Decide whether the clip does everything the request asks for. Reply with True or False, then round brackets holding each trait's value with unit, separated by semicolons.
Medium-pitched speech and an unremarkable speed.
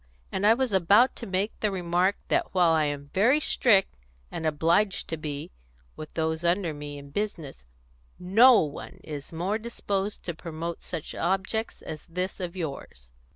True (175 Hz; 165 wpm)